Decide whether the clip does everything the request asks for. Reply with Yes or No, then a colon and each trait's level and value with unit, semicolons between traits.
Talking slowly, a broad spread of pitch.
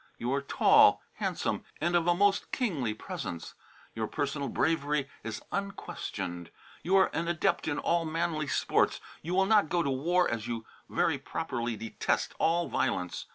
No: average, 165 wpm; wide, 6.5 semitones